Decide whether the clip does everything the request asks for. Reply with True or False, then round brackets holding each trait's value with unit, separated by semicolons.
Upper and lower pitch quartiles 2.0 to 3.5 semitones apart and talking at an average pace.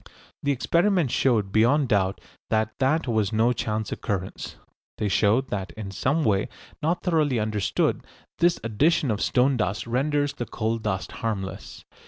False (5.2 semitones; 150 wpm)